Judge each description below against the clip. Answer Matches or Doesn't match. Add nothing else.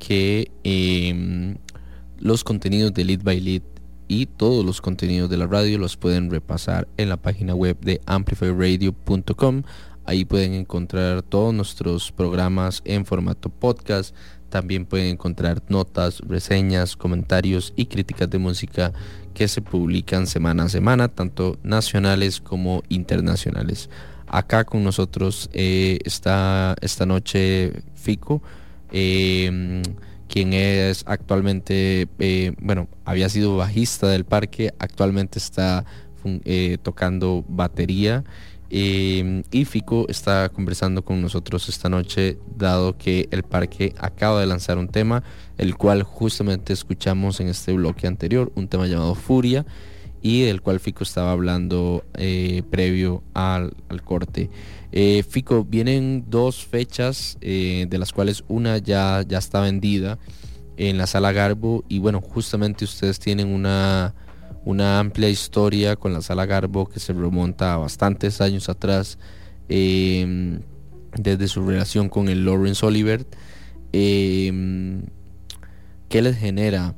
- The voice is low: Matches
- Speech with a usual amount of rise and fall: Doesn't match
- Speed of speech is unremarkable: Doesn't match